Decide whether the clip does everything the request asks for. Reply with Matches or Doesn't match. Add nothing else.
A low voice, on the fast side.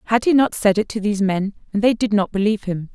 Doesn't match